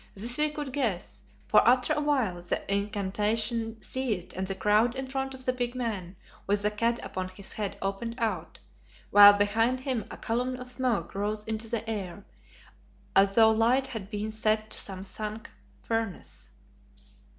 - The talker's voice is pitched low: No, high, 220 Hz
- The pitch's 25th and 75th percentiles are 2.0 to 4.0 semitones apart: Yes, average, 3.3 semitones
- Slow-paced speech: No, average, 165 wpm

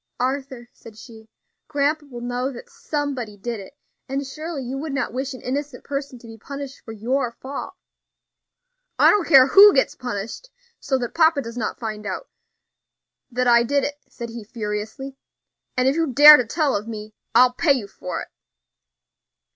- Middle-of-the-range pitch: No, very high, 255 Hz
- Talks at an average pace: Yes, average, 180 wpm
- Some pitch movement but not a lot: Yes, average, 3.4 semitones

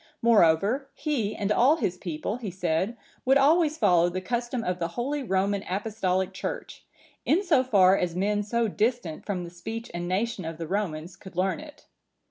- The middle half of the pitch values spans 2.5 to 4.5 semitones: No, average, 5.0 semitones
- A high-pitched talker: Yes, high, 200 Hz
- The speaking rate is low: No, average, 180 wpm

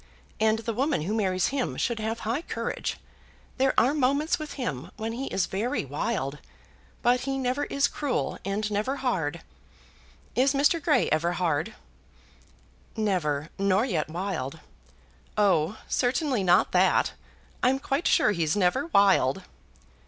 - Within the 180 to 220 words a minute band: No, average, 140 wpm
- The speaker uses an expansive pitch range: Yes, wide, 6.8 semitones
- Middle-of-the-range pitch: No, high, 220 Hz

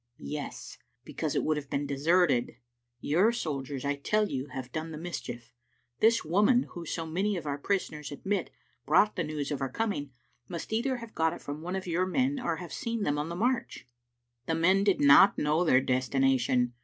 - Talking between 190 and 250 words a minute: Yes, average, 200 wpm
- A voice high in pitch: No, medium, 160 Hz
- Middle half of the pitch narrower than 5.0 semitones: No, wide, 5.6 semitones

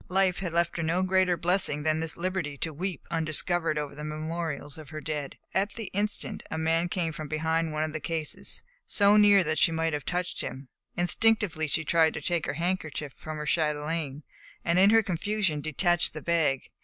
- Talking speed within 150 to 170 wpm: No, average, 200 wpm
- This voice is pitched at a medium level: Yes, medium, 165 Hz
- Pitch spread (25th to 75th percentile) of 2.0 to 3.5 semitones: Yes, average, 2.9 semitones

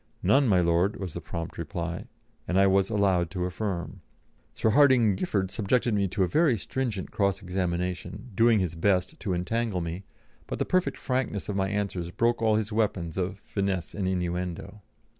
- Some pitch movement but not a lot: Yes, average, 3.4 semitones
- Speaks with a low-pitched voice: Yes, very low, 95 Hz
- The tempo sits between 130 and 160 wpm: No, average, 180 wpm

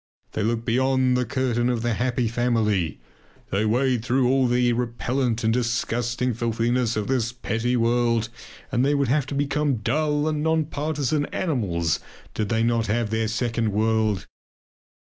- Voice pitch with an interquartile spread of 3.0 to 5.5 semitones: No, narrow, 2.6 semitones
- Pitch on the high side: No, low, 120 Hz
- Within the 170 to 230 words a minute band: No, average, 160 wpm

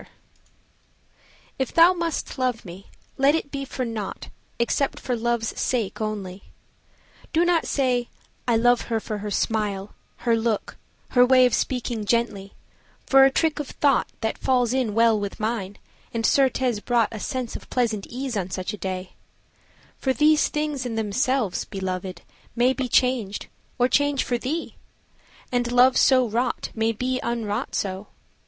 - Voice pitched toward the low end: No, high, 240 Hz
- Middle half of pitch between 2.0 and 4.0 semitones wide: Yes, average, 3.6 semitones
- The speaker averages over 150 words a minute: Yes, average, 160 wpm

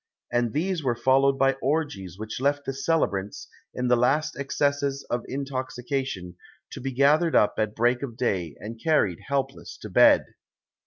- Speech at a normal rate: Yes, average, 160 wpm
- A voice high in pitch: No, low, 130 Hz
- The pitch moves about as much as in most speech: Yes, average, 3.4 semitones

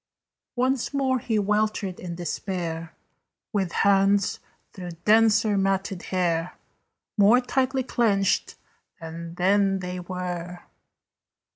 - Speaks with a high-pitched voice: Yes, high, 195 Hz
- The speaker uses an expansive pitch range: No, average, 3.3 semitones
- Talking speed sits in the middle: No, slow, 100 wpm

